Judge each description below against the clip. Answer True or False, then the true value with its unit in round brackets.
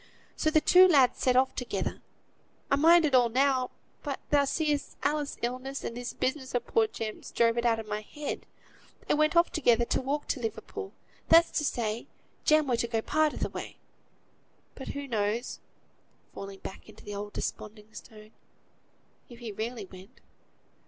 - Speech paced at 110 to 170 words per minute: False (180 wpm)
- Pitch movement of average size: True (4.7 semitones)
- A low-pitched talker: False (255 Hz)